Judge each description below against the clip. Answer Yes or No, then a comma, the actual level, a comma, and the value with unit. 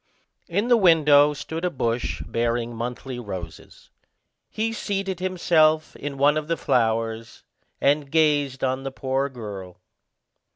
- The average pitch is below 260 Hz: Yes, medium, 140 Hz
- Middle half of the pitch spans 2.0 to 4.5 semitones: No, average, 5.3 semitones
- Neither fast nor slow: No, slow, 130 wpm